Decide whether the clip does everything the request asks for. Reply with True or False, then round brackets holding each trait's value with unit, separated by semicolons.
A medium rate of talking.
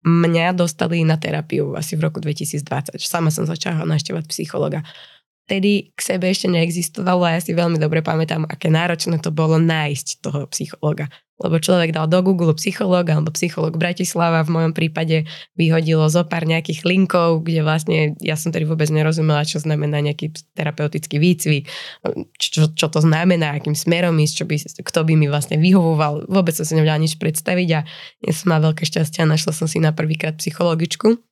False (180 wpm)